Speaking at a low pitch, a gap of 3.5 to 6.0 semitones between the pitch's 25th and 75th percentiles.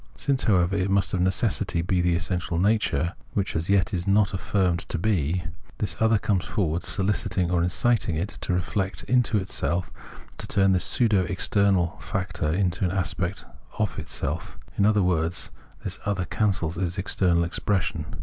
No: very low, 95 Hz; narrow, 2.6 semitones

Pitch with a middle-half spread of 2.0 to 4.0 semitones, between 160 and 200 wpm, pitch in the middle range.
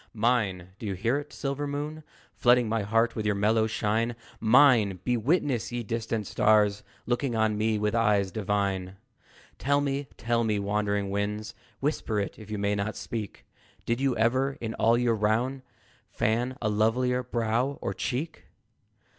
No: average, 3.0 semitones; average, 165 wpm; low, 115 Hz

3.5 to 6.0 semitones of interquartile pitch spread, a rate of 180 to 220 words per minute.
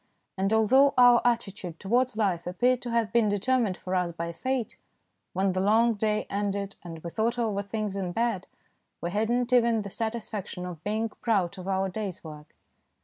Yes: average, 3.8 semitones; average, 185 wpm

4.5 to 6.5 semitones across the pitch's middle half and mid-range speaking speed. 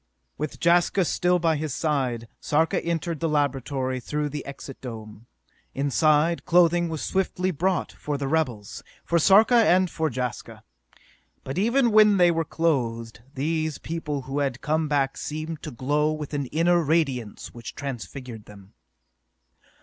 No: average, 4.0 semitones; average, 150 wpm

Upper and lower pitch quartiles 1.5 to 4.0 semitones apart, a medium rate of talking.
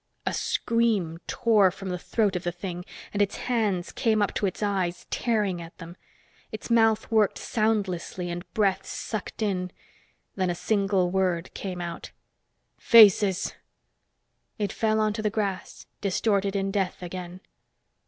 Yes: average, 3.0 semitones; average, 145 wpm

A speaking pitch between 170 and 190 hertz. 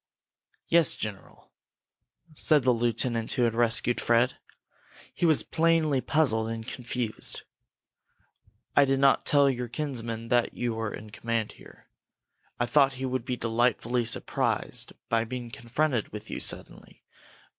No: low, 120 Hz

